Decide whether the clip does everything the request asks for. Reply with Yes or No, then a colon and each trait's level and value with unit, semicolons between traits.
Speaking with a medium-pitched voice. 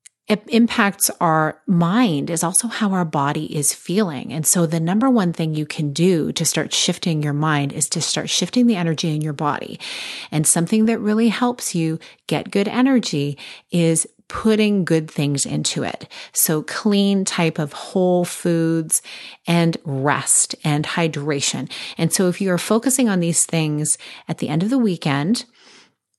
Yes: medium, 170 Hz